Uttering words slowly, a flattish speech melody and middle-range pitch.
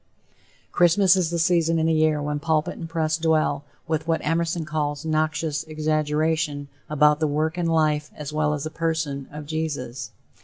No: average, 175 wpm; narrow, 1.5 semitones; medium, 155 Hz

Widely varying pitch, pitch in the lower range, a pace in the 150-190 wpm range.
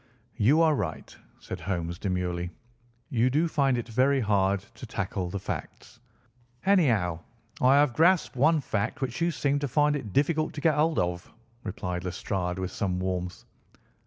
Yes: wide, 8.0 semitones; low, 115 Hz; average, 160 wpm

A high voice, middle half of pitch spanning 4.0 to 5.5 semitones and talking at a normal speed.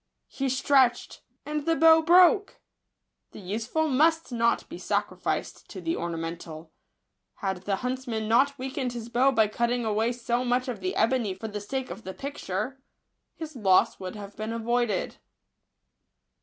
Yes: high, 240 Hz; average, 4.3 semitones; average, 160 wpm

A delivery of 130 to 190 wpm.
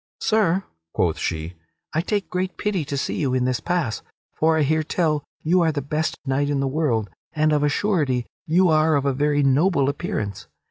No: average, 200 wpm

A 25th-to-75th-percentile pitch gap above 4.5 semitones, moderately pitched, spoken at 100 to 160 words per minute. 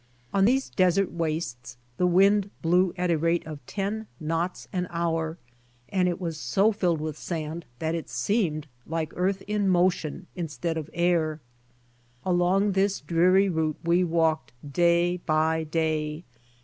No: narrow, 2.6 semitones; medium, 170 Hz; average, 150 wpm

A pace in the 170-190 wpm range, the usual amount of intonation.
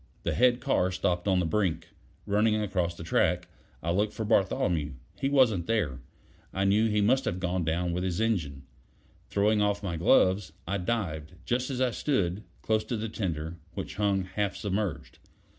Yes: average, 175 wpm; average, 3.9 semitones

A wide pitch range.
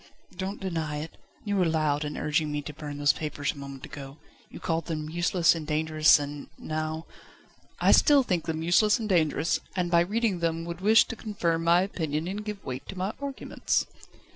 No: average, 3.7 semitones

